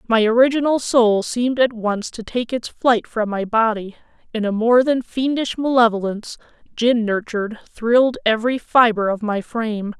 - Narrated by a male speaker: No, female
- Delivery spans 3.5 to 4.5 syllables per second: No, 4.9 syllables/s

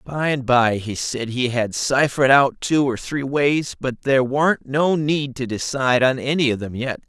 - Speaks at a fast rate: Yes, fast, 210 wpm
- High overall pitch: No, low, 130 Hz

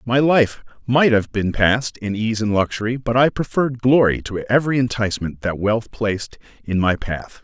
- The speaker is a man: Yes, male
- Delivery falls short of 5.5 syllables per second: Yes, 5.1 syllables/s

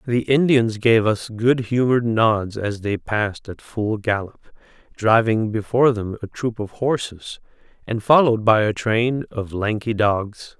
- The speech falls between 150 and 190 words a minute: Yes, average, 160 wpm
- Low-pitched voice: Yes, low, 110 Hz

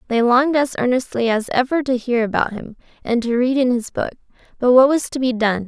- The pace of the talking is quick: Yes, fast, 230 wpm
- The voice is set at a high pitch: Yes, high, 245 Hz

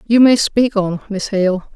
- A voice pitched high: Yes, high, 205 Hz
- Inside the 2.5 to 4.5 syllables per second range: Yes, 3.9 syllables/s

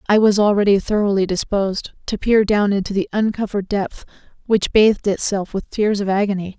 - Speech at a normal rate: Yes, average, 175 wpm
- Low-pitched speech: No, high, 200 Hz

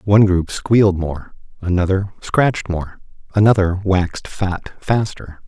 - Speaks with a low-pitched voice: Yes, very low, 95 Hz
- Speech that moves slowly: Yes, slow, 120 wpm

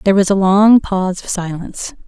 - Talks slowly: No, average, 200 wpm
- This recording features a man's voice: No, female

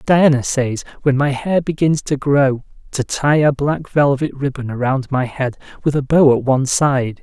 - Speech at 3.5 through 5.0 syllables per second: Yes, 4.5 syllables/s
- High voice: No, medium, 140 Hz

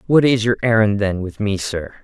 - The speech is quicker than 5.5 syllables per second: No, 5.1 syllables/s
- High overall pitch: No, low, 105 Hz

